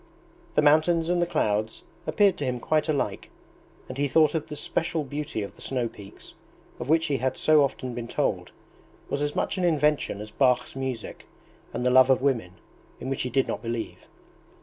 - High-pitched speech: No, low, 135 Hz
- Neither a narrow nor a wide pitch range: Yes, average, 3.8 semitones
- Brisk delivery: No, average, 195 wpm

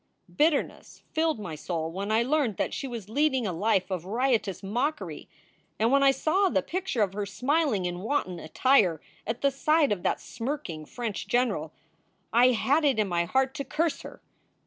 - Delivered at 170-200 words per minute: Yes, average, 185 wpm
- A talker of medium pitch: No, high, 235 Hz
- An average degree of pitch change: No, wide, 6.4 semitones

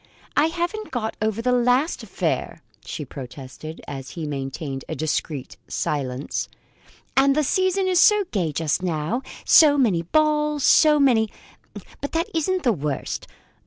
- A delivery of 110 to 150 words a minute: Yes, average, 145 wpm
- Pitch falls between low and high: No, high, 235 Hz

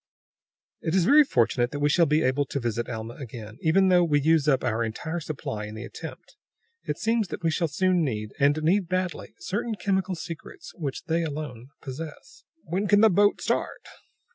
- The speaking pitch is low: No, medium, 160 Hz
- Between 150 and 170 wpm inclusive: No, average, 190 wpm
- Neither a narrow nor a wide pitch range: No, wide, 6.1 semitones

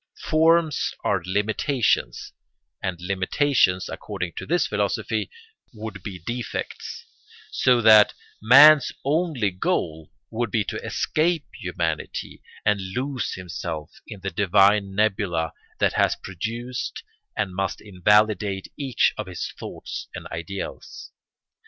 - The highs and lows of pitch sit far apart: No, average, 4.7 semitones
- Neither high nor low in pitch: No, low, 105 Hz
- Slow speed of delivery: Yes, slow, 115 wpm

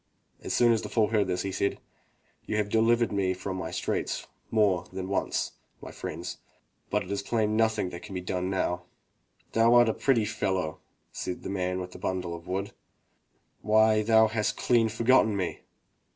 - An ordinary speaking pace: Yes, average, 185 wpm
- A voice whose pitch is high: No, low, 100 Hz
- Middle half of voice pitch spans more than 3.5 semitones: No, average, 3.2 semitones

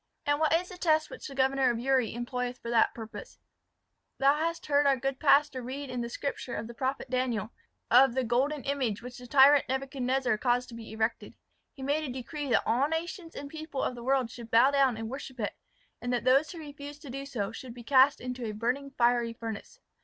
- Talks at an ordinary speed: No, fast, 220 wpm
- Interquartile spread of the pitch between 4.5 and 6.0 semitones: No, average, 2.9 semitones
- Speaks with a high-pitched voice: Yes, very high, 260 Hz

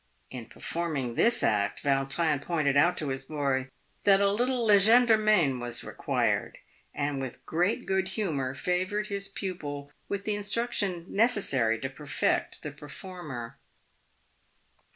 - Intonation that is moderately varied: No, wide, 6.8 semitones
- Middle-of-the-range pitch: Yes, medium, 170 Hz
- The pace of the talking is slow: Yes, slow, 130 wpm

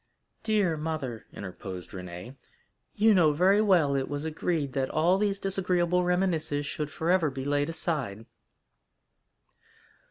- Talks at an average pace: No, slow, 125 wpm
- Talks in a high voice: No, medium, 160 Hz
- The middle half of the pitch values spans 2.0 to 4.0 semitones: No, average, 4.8 semitones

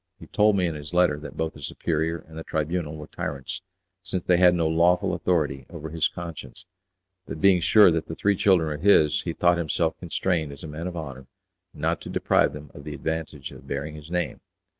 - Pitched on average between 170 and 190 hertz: No, very low, 80 Hz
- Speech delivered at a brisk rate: Yes, fast, 215 wpm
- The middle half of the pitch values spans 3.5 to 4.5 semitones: No, average, 2.7 semitones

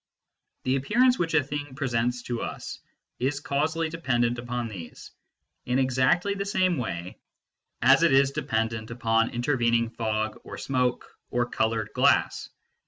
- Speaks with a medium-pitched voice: No, low, 125 Hz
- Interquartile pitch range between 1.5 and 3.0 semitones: No, average, 3.9 semitones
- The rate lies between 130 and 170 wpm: Yes, average, 145 wpm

